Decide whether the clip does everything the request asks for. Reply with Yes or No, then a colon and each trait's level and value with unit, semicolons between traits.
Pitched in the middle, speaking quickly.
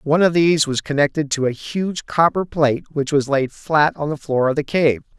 Yes: medium, 150 Hz; fast, 230 wpm